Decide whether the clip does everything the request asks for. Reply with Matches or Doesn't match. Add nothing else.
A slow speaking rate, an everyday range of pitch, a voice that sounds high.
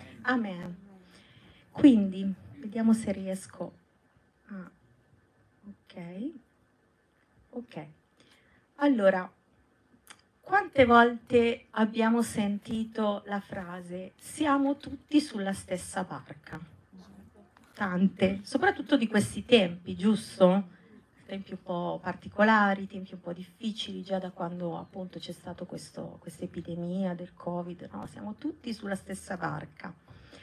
Matches